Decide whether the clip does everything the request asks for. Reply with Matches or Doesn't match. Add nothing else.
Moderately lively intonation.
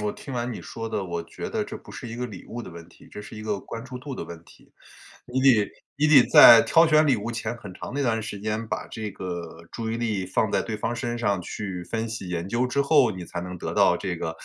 Matches